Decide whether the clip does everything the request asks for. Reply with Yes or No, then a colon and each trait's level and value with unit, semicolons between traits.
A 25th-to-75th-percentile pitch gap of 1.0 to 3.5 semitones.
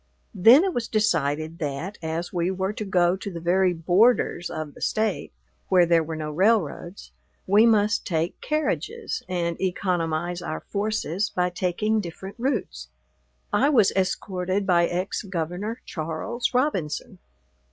No: average, 4.0 semitones